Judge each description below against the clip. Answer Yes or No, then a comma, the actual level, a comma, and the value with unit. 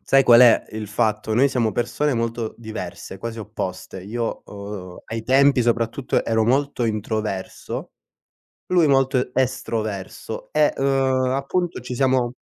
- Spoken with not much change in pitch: No, average, 3.4 semitones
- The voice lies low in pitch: Yes, low, 120 Hz